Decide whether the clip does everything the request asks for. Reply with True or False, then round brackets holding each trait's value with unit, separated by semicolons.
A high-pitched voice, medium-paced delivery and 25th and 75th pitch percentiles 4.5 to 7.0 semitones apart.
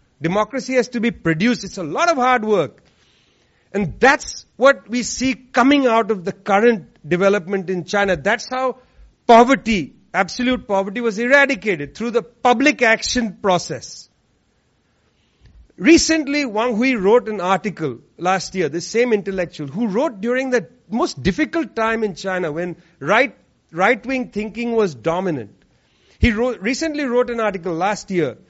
True (220 Hz; 150 wpm; 4.8 semitones)